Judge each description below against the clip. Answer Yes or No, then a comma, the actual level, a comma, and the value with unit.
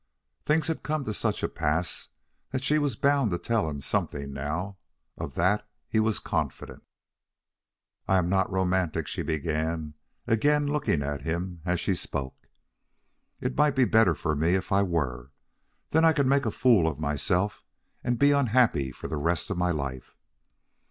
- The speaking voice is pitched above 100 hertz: No, very low, 95 Hz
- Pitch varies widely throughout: Yes, wide, 8.3 semitones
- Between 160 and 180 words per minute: Yes, average, 170 wpm